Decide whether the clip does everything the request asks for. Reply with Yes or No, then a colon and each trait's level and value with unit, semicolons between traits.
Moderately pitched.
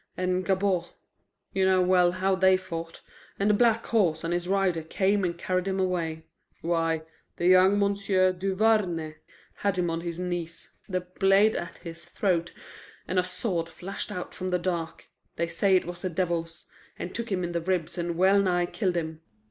Yes: medium, 180 Hz